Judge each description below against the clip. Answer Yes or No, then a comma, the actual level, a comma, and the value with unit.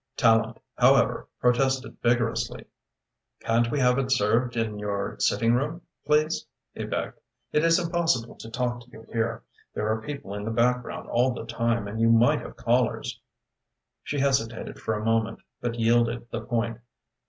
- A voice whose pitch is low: Yes, low, 120 Hz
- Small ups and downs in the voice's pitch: Yes, narrow, 2.1 semitones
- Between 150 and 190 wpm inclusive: Yes, average, 165 wpm